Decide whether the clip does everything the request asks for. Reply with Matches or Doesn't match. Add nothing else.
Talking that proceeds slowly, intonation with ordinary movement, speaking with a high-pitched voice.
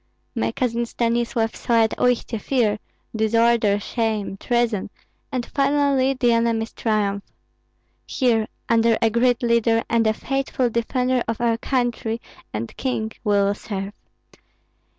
Doesn't match